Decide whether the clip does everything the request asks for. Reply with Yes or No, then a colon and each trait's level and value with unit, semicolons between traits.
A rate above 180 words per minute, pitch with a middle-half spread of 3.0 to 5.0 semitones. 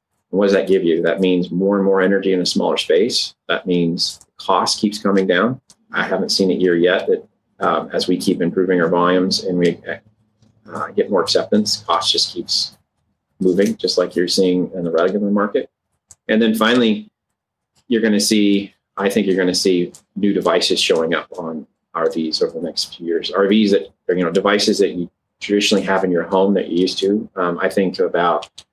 No: fast, 205 wpm; narrow, 2.6 semitones